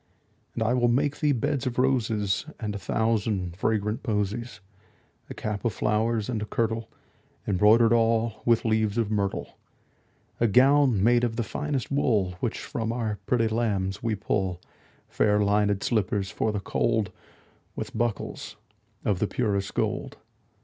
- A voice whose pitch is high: No, low, 110 Hz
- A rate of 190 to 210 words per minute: No, average, 155 wpm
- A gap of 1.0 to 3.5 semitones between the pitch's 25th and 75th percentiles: Yes, narrow, 2.4 semitones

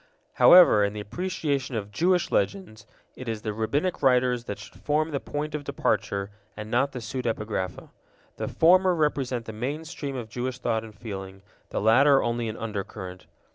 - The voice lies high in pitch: No, low, 120 Hz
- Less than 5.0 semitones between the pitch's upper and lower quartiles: No, average, 5.3 semitones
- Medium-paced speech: Yes, average, 175 wpm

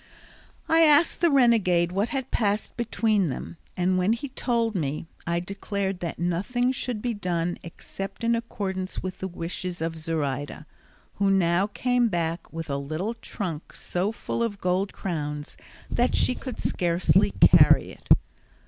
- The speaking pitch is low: No, high, 190 Hz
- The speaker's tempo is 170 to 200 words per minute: No, average, 155 wpm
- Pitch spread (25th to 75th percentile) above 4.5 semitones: Yes, average, 5.3 semitones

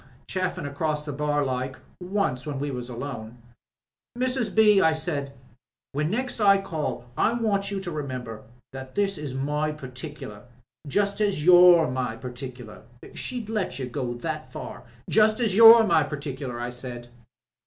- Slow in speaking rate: No, average, 165 wpm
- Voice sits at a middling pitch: Yes, medium, 150 Hz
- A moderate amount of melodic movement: No, wide, 7.3 semitones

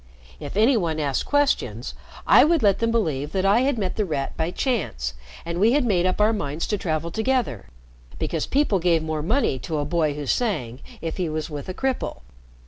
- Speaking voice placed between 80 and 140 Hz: No, medium, 180 Hz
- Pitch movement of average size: No, wide, 6.7 semitones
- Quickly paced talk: Yes, fast, 210 wpm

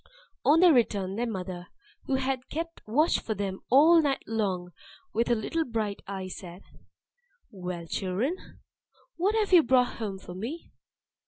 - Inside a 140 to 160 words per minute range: Yes, average, 155 wpm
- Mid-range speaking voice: No, high, 225 Hz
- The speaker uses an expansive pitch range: Yes, wide, 7.2 semitones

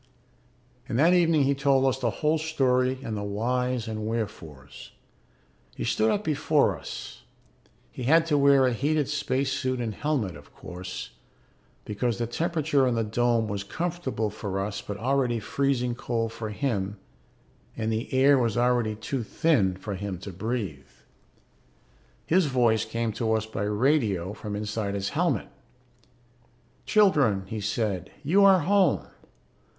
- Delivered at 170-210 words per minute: No, average, 150 wpm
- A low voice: Yes, low, 120 Hz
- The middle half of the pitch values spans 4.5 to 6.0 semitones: Yes, average, 4.9 semitones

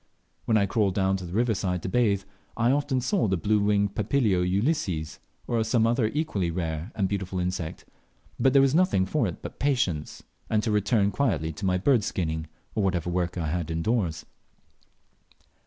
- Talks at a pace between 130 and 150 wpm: No, average, 190 wpm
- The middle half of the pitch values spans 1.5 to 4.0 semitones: No, average, 4.7 semitones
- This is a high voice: No, low, 100 Hz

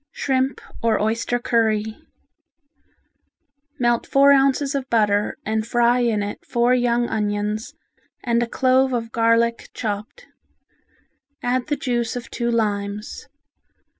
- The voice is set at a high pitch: Yes, high, 235 Hz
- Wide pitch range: No, narrow, 2.4 semitones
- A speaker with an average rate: No, slow, 120 wpm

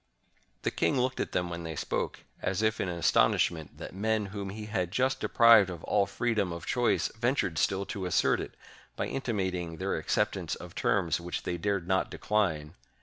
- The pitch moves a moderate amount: Yes, average, 3.9 semitones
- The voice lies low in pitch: Yes, very low, 95 Hz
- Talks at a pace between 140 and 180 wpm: No, average, 190 wpm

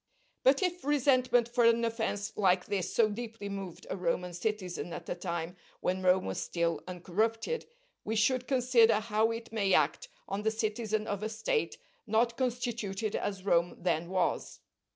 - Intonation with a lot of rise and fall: No, average, 4.2 semitones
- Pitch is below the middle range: No, high, 215 Hz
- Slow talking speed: No, average, 165 wpm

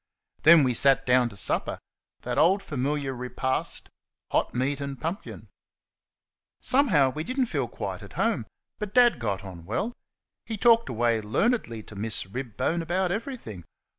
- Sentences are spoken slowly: No, average, 155 wpm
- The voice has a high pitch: No, medium, 140 Hz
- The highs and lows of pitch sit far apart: Yes, wide, 8.6 semitones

